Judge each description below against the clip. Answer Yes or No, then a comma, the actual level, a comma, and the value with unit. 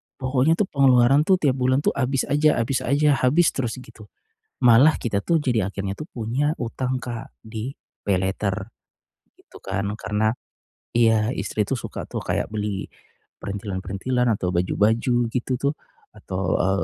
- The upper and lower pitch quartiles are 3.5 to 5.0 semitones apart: Yes, average, 4.5 semitones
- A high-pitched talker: No, low, 120 Hz